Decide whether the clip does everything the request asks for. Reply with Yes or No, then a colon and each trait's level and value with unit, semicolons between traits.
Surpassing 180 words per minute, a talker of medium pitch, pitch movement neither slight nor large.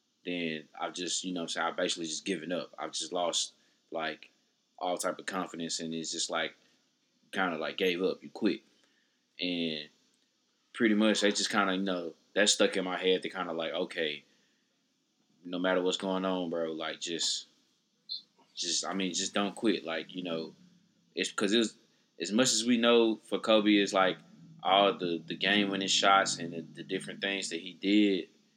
No: average, 195 wpm; very low, 95 Hz; average, 3.0 semitones